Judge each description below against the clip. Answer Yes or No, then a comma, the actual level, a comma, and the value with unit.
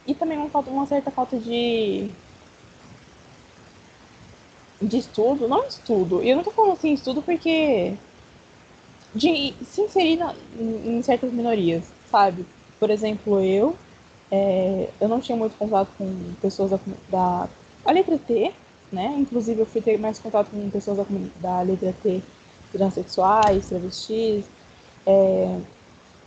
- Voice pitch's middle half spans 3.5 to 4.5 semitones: No, average, 5.2 semitones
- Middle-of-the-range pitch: No, high, 220 Hz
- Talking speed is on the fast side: No, average, 135 wpm